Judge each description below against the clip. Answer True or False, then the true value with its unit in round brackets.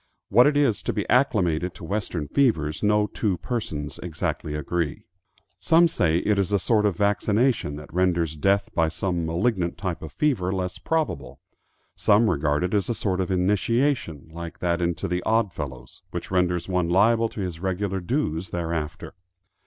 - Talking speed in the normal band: True (170 wpm)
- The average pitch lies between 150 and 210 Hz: False (90 Hz)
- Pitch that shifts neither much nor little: True (4.0 semitones)